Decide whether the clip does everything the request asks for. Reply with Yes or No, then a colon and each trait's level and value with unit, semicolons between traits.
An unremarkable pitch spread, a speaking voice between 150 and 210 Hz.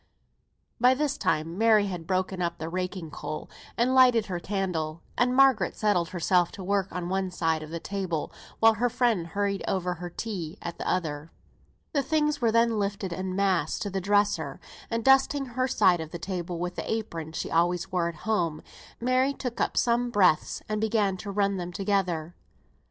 Yes: average, 4.5 semitones; high, 190 Hz